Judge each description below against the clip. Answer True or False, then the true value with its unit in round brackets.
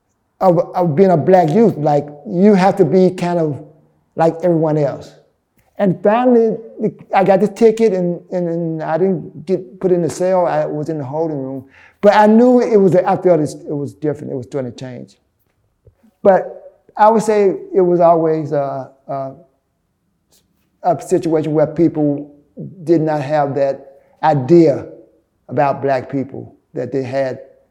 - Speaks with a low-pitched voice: False (165 Hz)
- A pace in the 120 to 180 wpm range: True (165 wpm)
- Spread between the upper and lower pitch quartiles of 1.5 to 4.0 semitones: False (4.6 semitones)